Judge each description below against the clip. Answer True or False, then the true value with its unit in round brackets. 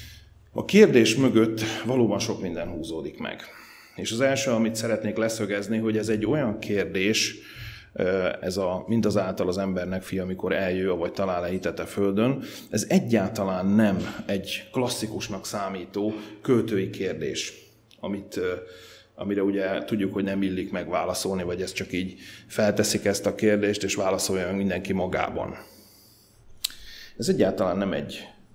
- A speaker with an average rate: True (140 wpm)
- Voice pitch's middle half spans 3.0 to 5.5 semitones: False (2.4 semitones)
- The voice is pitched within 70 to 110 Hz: True (100 Hz)